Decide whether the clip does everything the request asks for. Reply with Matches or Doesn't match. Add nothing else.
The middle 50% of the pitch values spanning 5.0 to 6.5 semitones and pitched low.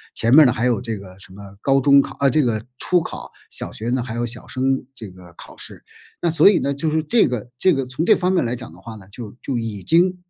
Matches